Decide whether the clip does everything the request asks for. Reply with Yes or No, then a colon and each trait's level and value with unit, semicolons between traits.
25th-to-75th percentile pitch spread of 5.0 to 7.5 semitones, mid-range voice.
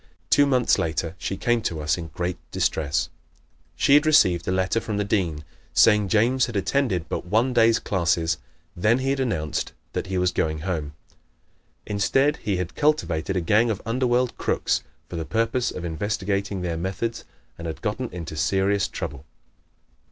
No: wide, 5.5 semitones; low, 100 Hz